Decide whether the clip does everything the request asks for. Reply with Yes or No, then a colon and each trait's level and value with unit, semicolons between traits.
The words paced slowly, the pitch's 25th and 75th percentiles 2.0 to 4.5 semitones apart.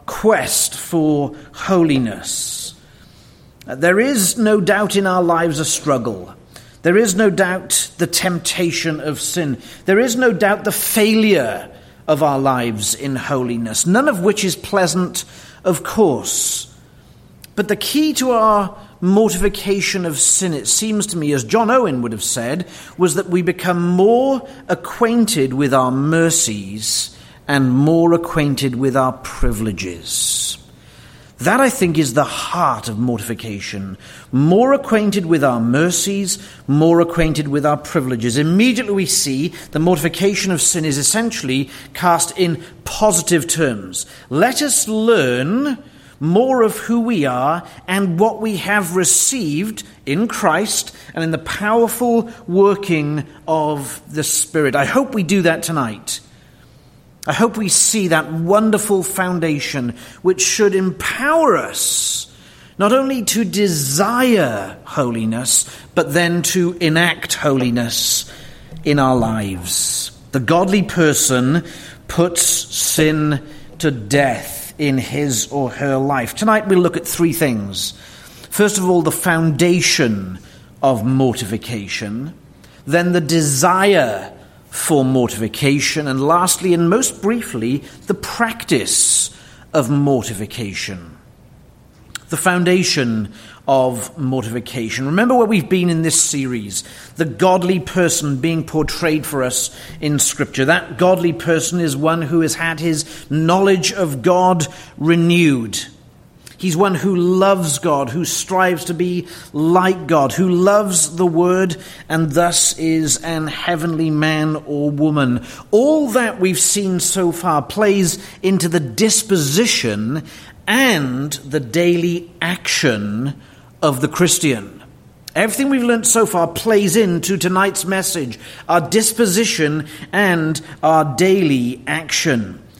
No: slow, 125 wpm; wide, 5.4 semitones